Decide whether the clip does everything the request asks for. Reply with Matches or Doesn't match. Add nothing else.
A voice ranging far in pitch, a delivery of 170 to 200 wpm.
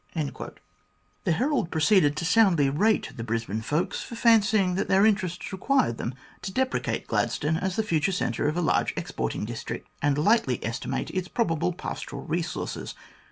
Matches